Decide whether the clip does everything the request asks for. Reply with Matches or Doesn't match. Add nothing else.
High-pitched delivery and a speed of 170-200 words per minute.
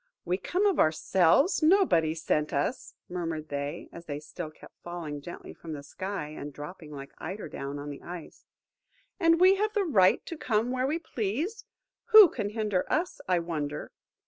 Doesn't match